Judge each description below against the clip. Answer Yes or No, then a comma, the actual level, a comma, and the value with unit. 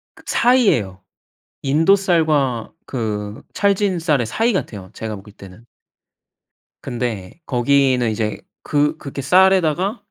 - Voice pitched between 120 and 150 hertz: Yes, medium, 140 Hz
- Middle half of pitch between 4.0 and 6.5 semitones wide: No, wide, 8.8 semitones